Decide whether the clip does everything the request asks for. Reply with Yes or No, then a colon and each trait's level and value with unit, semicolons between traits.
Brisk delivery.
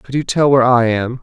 Yes: fast, 295 wpm